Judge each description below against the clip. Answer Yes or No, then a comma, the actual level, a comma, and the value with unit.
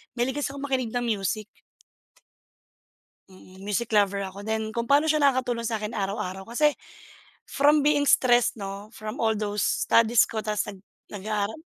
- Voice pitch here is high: Yes, high, 220 Hz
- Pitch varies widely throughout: No, average, 3.7 semitones